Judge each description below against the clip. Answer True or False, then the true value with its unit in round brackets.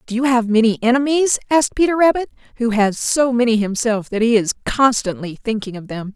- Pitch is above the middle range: True (235 Hz)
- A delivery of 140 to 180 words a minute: False (195 wpm)